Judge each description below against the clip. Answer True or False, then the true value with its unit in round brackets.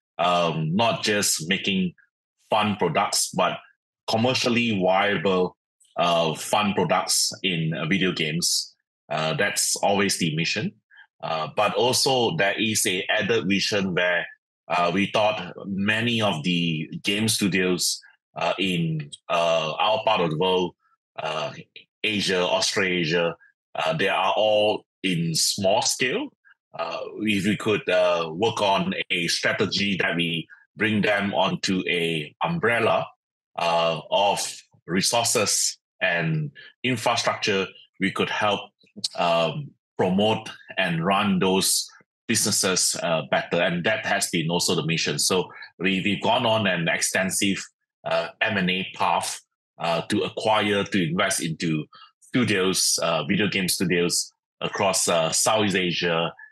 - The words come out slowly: True (125 wpm)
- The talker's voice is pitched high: False (95 Hz)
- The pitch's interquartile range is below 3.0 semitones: False (3.8 semitones)